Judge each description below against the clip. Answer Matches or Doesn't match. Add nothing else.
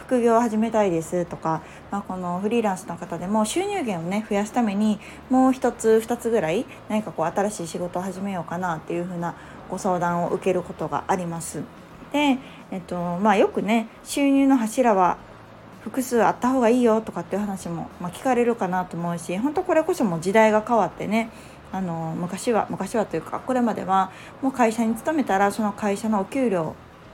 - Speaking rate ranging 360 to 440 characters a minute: Matches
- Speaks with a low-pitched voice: Doesn't match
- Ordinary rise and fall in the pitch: Matches